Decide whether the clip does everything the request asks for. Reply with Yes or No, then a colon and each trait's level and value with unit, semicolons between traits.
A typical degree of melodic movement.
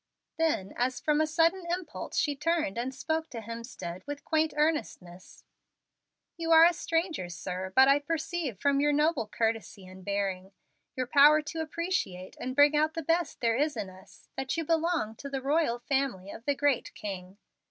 No: wide, 7.0 semitones